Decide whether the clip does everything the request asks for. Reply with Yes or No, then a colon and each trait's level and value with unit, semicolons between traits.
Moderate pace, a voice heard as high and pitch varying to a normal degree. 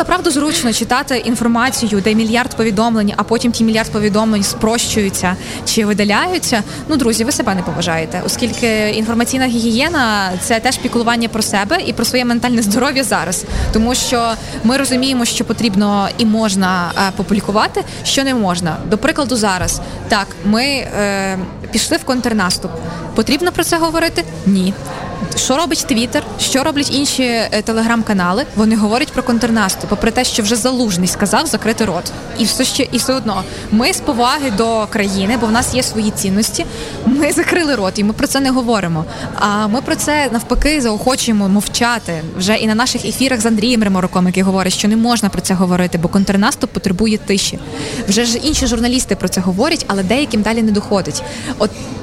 No: fast, 170 wpm; high, 225 Hz; average, 3.8 semitones